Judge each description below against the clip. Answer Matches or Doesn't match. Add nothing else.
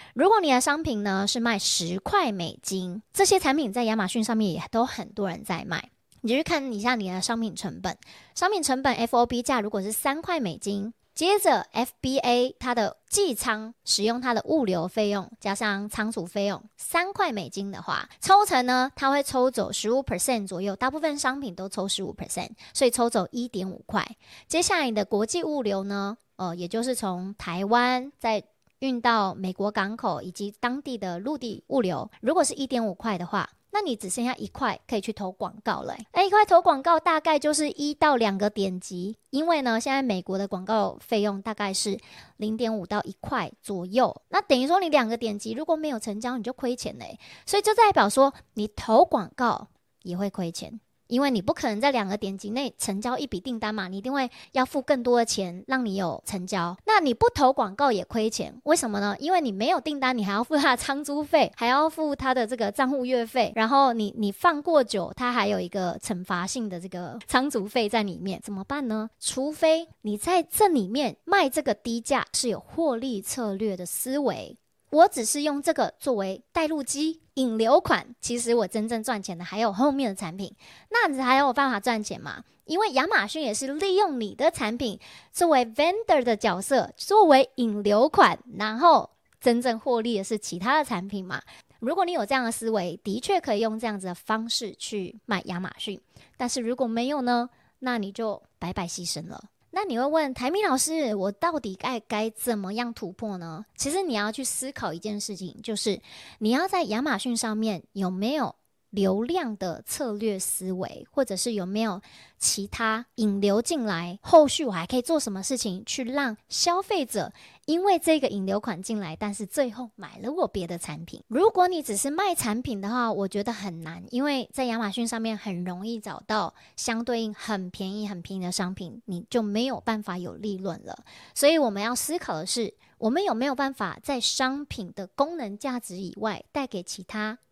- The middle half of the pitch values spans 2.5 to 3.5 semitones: Doesn't match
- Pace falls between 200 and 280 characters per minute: Doesn't match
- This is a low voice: Doesn't match